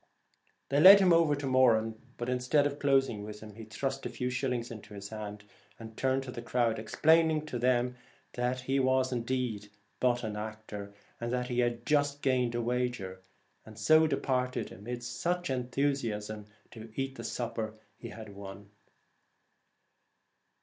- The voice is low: Yes, low, 125 Hz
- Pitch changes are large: No, average, 3.5 semitones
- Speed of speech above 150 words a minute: Yes, average, 170 wpm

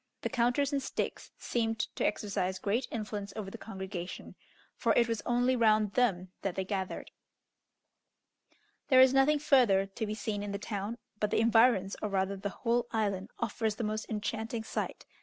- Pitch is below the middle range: No, high, 215 Hz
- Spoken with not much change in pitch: No, average, 3.1 semitones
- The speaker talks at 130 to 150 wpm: No, average, 175 wpm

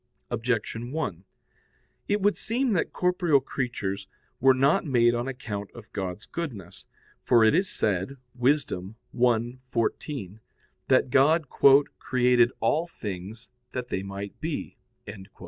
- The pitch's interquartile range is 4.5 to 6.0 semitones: Yes, average, 5.1 semitones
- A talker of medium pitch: No, low, 125 Hz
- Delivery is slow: Yes, slow, 120 wpm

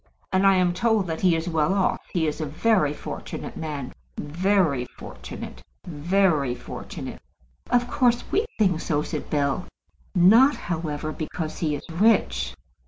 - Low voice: No, medium, 170 Hz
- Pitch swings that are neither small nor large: Yes, average, 4.6 semitones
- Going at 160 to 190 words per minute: No, average, 150 wpm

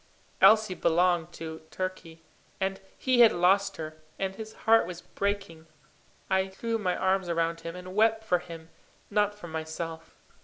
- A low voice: No, medium, 185 Hz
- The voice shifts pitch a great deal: No, average, 3.4 semitones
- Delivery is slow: No, average, 155 wpm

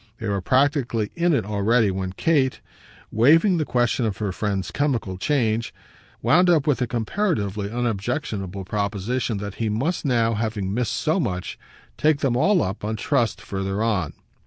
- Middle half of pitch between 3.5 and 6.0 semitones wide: Yes, wide, 5.6 semitones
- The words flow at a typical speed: Yes, average, 160 wpm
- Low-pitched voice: Yes, low, 115 Hz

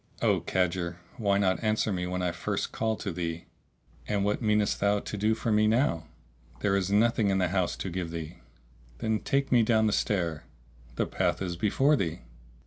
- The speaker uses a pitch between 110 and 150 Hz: No, low, 100 Hz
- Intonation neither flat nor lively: Yes, average, 3.4 semitones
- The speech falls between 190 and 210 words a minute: Yes, average, 195 wpm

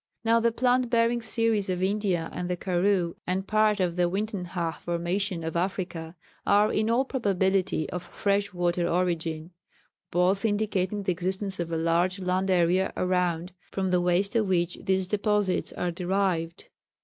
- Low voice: No, medium, 185 Hz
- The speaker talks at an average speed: Yes, average, 160 wpm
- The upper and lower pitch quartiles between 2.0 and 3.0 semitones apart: Yes, average, 2.7 semitones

